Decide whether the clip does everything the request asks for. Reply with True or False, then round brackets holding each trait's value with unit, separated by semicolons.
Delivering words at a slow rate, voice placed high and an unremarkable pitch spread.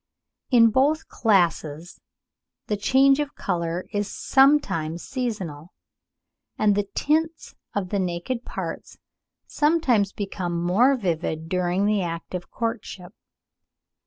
False (110 wpm; 200 Hz; 6.5 semitones)